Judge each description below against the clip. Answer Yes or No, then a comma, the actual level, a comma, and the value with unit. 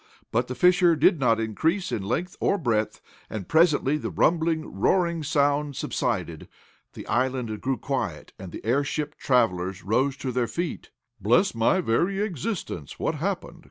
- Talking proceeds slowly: No, average, 155 wpm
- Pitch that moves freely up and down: Yes, wide, 6.8 semitones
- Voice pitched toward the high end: No, medium, 140 Hz